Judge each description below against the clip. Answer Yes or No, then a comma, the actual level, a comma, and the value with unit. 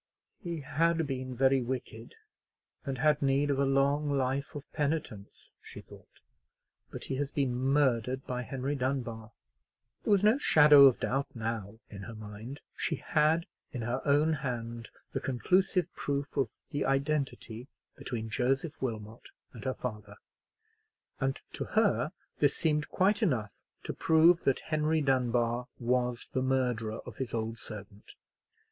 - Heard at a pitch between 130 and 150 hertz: Yes, low, 135 Hz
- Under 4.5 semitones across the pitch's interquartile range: Yes, average, 3.8 semitones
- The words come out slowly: No, average, 150 wpm